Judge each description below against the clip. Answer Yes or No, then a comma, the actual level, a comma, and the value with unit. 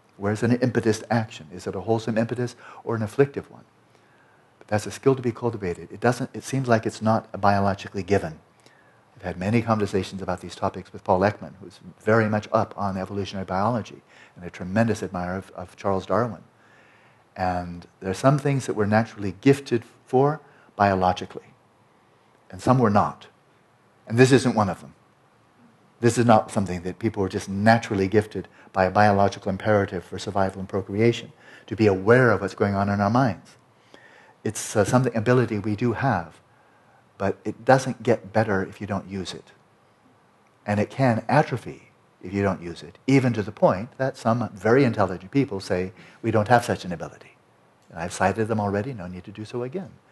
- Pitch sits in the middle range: No, low, 105 Hz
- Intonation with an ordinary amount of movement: Yes, average, 3.6 semitones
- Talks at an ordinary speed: Yes, average, 190 wpm